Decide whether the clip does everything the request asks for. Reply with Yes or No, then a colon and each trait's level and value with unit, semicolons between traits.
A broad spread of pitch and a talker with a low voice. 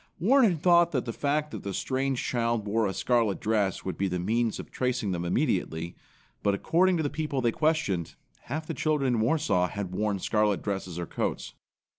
Yes: wide, 7.1 semitones; low, 115 Hz